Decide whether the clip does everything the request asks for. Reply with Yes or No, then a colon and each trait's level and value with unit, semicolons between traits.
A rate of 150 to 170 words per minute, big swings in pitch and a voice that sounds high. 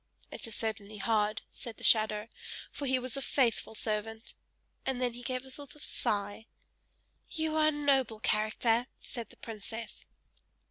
No: average, 160 wpm; average, 3.3 semitones; high, 230 Hz